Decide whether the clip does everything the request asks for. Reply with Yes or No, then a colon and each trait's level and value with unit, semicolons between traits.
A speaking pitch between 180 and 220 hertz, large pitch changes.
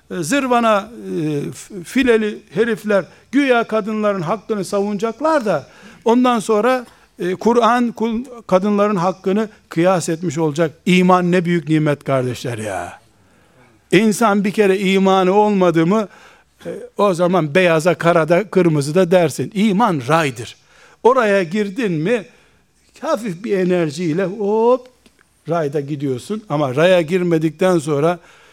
No: high, 190 Hz; average, 4.5 semitones